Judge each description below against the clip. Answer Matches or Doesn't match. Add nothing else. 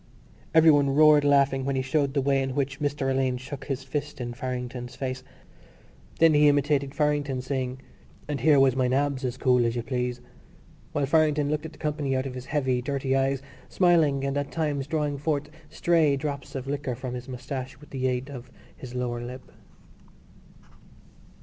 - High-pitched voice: Doesn't match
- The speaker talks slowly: Doesn't match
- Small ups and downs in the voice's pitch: Matches